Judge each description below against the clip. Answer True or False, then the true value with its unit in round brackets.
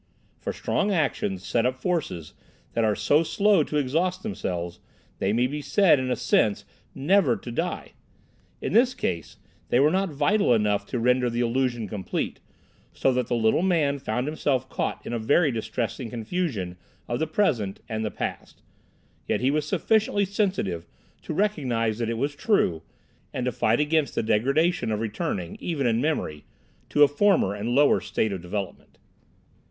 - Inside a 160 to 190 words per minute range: True (170 wpm)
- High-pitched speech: False (125 Hz)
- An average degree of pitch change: False (6.4 semitones)